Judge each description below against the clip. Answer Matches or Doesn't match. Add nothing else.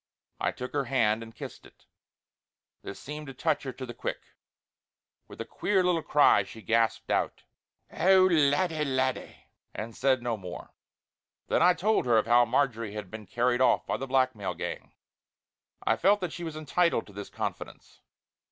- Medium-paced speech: Matches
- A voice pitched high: Doesn't match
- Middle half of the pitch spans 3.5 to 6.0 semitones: Matches